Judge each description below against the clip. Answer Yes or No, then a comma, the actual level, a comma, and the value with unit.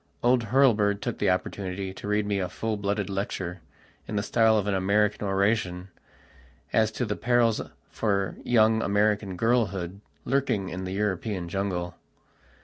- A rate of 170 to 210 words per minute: No, average, 150 wpm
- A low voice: Yes, low, 100 Hz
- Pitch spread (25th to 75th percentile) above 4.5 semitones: No, narrow, 2.4 semitones